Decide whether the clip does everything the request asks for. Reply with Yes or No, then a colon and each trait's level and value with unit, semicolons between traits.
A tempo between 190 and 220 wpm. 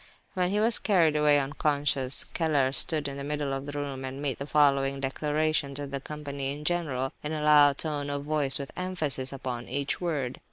Yes: average, 200 wpm